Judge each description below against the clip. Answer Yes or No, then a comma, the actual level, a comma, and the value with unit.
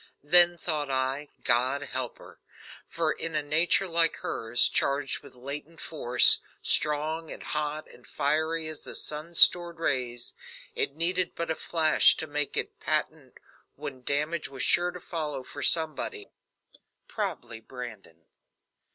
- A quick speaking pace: No, average, 145 wpm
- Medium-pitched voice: Yes, medium, 150 Hz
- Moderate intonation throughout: Yes, average, 3.7 semitones